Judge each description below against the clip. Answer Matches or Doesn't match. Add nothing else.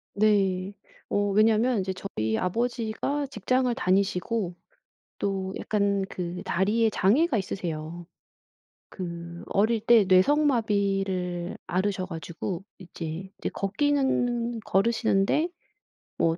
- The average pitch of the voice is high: Matches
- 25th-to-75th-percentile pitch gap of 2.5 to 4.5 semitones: Matches